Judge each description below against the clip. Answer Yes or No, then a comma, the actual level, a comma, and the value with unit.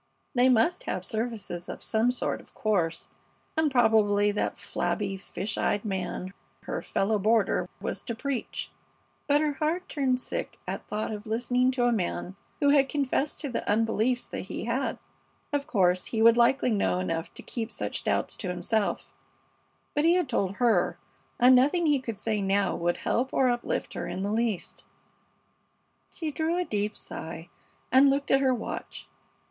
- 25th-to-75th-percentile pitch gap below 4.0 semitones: No, average, 4.7 semitones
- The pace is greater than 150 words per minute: Yes, average, 175 wpm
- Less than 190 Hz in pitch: No, high, 230 Hz